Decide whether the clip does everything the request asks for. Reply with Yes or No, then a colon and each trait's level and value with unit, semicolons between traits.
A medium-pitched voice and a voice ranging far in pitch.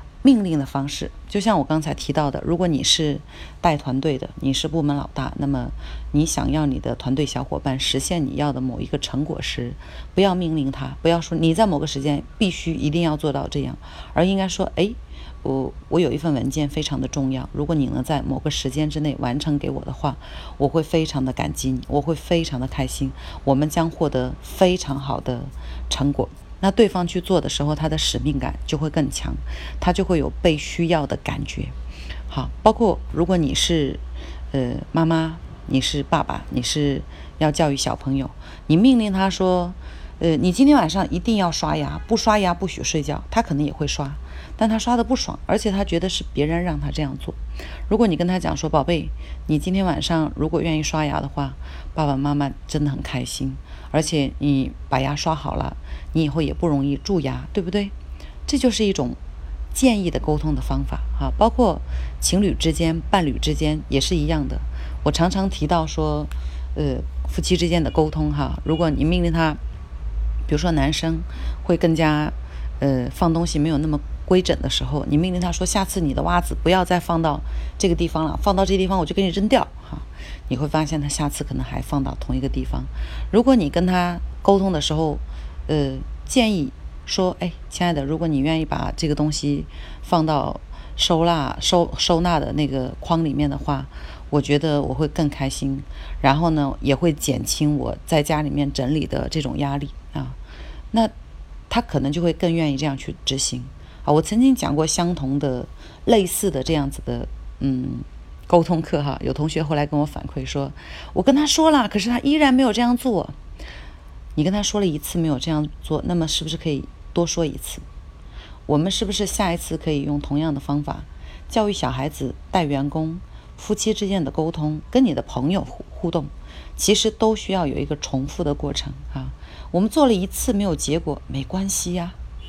No: medium, 150 Hz; average, 4.2 semitones